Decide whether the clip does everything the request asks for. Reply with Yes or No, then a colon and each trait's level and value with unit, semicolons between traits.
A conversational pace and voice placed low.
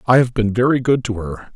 No: fast, 270 wpm; low, 115 Hz